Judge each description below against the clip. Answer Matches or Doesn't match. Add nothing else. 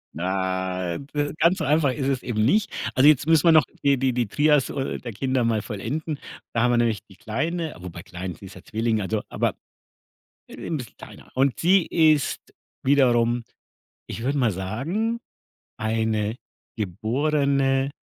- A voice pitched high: Doesn't match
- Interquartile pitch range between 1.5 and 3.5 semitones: Doesn't match